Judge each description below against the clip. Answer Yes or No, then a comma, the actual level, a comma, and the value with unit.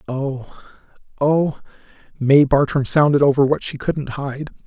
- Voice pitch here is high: No, medium, 140 Hz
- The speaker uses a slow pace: Yes, slow, 130 wpm